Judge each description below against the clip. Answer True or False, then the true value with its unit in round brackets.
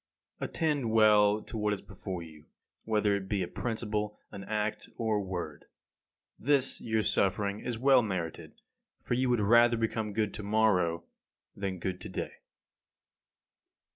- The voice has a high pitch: False (105 Hz)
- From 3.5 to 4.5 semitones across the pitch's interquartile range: False (2.5 semitones)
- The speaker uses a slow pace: False (160 wpm)